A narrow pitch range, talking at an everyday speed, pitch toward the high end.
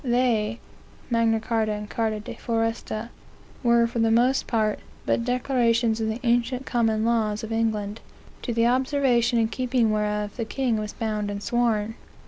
Yes: narrow, 1.8 semitones; average, 160 wpm; high, 230 Hz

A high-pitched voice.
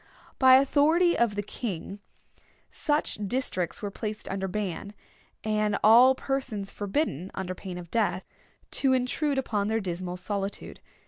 Yes: high, 210 Hz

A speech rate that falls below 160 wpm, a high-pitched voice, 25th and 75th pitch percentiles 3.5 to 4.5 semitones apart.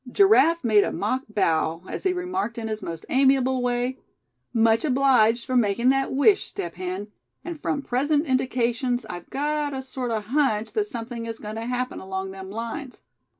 No: average, 180 wpm; high, 245 Hz; average, 4.0 semitones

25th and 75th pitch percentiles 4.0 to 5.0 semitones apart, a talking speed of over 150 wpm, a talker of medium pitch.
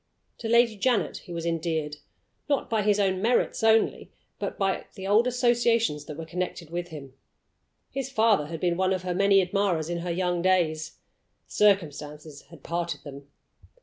Yes: average, 4.4 semitones; average, 165 wpm; medium, 180 Hz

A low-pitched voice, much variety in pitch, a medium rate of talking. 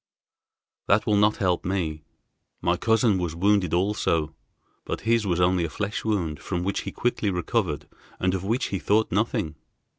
No: very low, 95 Hz; average, 3.3 semitones; average, 170 wpm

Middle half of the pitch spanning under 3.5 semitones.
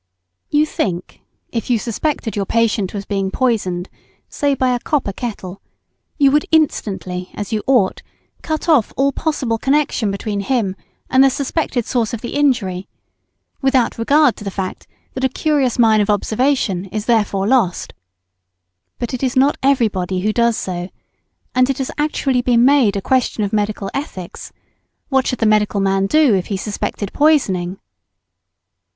No: average, 5.2 semitones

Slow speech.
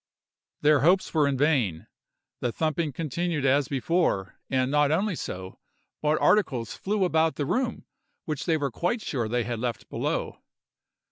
No: average, 145 wpm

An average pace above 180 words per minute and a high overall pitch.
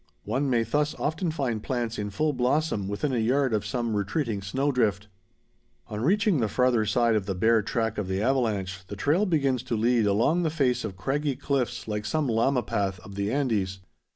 No: average, 200 wpm; low, 120 Hz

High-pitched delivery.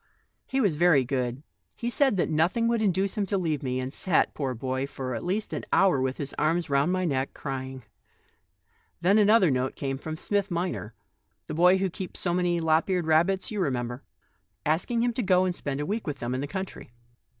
No: medium, 165 Hz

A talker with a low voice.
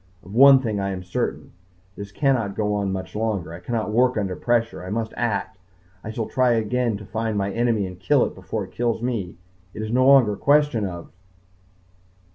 Yes: low, 110 Hz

